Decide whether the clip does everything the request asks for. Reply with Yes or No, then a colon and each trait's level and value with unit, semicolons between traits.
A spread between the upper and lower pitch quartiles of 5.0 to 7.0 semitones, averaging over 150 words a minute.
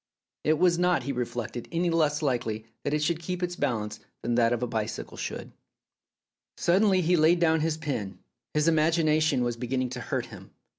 Yes: wide, 5.4 semitones; average, 180 wpm